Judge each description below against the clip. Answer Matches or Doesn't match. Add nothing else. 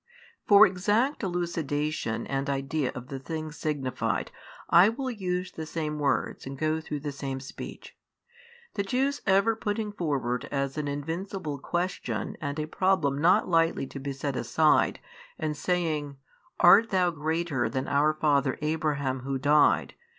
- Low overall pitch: Doesn't match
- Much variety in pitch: Doesn't match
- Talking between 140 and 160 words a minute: Matches